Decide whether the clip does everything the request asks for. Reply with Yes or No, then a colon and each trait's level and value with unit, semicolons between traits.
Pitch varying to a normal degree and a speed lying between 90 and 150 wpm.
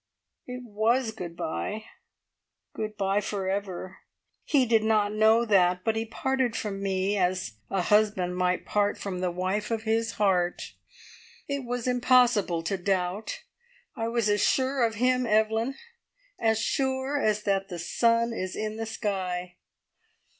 Yes: average, 3.5 semitones; average, 145 wpm